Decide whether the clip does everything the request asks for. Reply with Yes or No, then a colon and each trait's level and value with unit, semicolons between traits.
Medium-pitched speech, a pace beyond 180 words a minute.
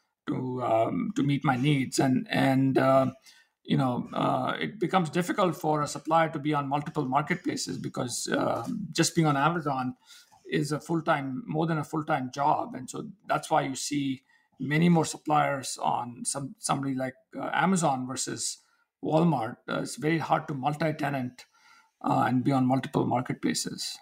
No: medium, 150 Hz; average, 165 wpm